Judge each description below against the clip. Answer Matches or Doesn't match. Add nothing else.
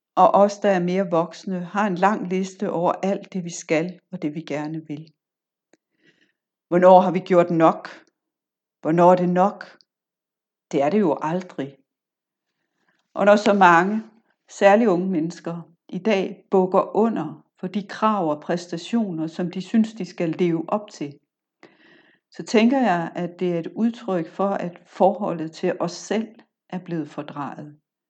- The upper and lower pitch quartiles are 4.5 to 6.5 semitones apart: Doesn't match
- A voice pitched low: Doesn't match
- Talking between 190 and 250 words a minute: Doesn't match